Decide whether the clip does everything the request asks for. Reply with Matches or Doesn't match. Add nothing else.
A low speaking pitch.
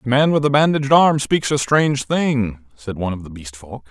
Matches